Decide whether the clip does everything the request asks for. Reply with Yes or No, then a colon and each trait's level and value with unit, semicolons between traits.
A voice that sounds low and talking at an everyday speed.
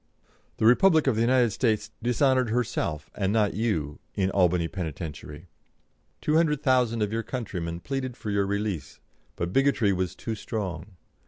Yes: low, 105 Hz; average, 155 wpm